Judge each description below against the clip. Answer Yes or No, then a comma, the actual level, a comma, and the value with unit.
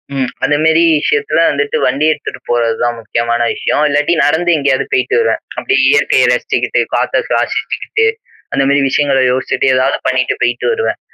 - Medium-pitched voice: Yes, medium, 145 Hz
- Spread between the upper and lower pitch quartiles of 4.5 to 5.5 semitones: Yes, average, 5.2 semitones